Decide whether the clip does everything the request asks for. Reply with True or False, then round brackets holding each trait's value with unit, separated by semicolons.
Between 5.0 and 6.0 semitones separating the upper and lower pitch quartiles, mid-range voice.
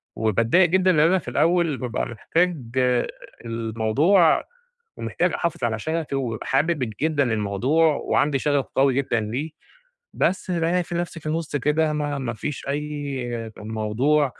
True (5.6 semitones; 145 Hz)